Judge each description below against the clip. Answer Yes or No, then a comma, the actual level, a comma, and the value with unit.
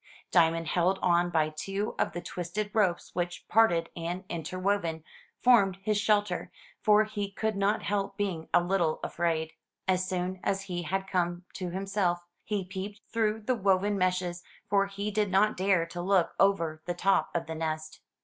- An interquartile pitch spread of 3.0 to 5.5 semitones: No, narrow, 2.6 semitones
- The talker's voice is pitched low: No, medium, 185 Hz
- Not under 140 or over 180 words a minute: Yes, average, 170 wpm